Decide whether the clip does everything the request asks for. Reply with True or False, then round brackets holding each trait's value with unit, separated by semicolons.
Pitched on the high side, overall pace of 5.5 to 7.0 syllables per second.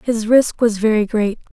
False (220 Hz; 4.6 syllables/s)